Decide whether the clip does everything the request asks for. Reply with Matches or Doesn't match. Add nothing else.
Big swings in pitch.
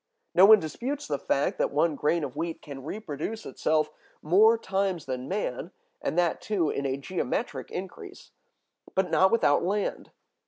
Matches